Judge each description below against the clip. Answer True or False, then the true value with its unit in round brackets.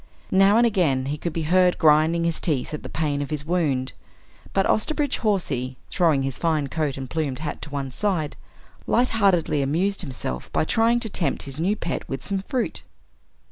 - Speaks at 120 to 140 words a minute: False (185 wpm)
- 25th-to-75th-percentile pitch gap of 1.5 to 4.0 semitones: False (5.4 semitones)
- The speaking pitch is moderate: True (160 Hz)